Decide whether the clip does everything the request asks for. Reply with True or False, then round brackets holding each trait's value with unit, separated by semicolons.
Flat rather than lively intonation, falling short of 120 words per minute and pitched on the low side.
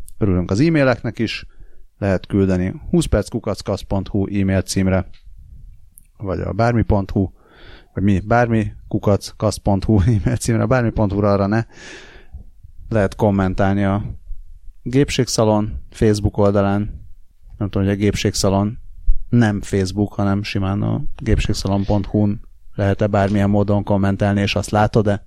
True (2.1 semitones; 110 wpm; 100 Hz)